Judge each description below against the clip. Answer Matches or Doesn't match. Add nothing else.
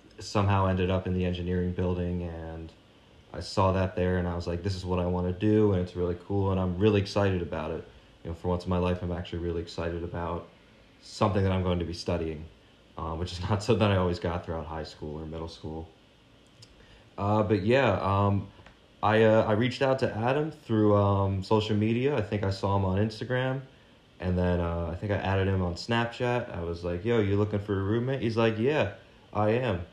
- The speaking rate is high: Matches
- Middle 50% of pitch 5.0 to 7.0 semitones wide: Doesn't match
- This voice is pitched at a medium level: Doesn't match